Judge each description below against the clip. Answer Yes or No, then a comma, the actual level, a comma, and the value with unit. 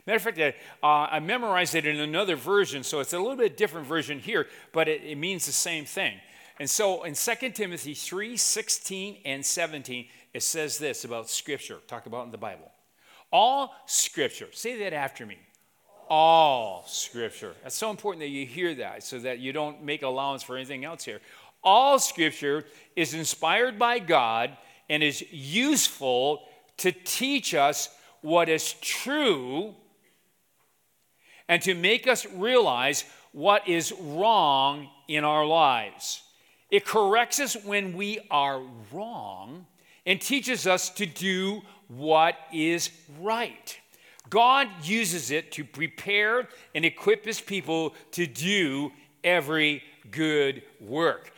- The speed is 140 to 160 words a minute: Yes, average, 145 wpm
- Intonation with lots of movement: Yes, wide, 6.2 semitones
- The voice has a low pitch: No, medium, 170 Hz